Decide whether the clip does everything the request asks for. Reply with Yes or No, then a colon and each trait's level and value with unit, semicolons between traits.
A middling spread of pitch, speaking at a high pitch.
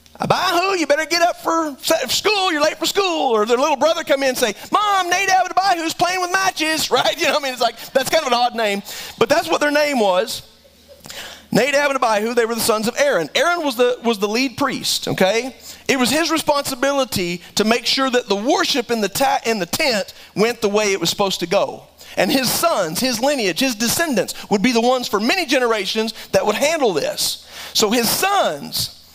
No: wide, 5.9 semitones; very high, 265 Hz